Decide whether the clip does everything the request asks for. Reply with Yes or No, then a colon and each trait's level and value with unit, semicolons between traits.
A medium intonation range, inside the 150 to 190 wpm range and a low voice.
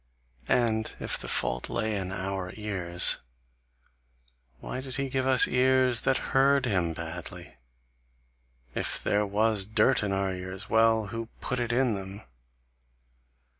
No: average, 4.8 semitones; slow, 135 wpm; low, 110 Hz